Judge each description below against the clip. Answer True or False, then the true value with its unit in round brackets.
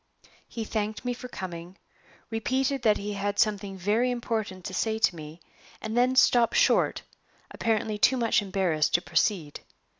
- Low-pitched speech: False (210 Hz)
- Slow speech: False (155 wpm)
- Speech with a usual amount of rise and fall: True (3.7 semitones)